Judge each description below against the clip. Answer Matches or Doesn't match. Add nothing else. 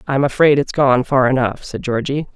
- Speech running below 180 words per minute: Doesn't match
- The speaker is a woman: Matches